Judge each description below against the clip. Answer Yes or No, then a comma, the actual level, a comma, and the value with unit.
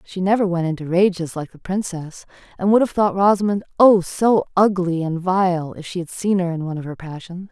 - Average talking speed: No, fast, 215 wpm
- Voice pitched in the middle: Yes, medium, 180 Hz